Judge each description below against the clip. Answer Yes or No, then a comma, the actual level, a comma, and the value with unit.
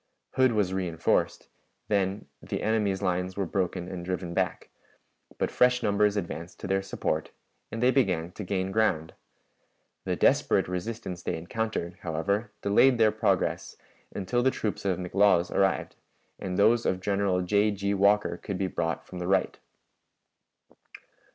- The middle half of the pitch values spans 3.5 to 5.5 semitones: No, narrow, 2.6 semitones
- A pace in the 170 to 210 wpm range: No, average, 150 wpm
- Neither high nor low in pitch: No, very low, 95 Hz